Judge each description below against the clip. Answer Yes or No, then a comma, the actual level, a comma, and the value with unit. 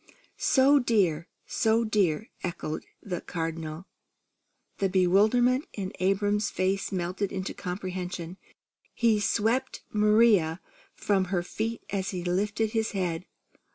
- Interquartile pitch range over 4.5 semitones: No, average, 3.4 semitones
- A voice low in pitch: No, high, 195 Hz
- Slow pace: Yes, slow, 115 wpm